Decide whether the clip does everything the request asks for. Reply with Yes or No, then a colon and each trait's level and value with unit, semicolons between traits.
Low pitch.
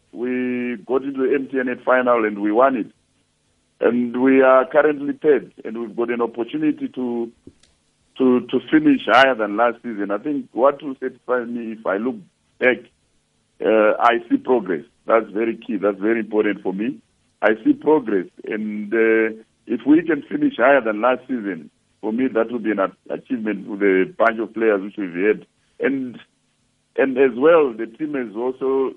Yes: low, 125 Hz